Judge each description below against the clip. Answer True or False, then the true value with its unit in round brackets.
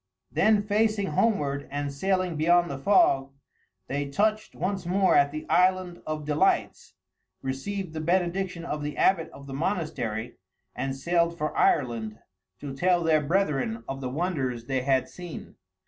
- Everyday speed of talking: True (150 wpm)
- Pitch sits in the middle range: True (155 Hz)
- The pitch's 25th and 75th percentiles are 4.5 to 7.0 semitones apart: True (5.0 semitones)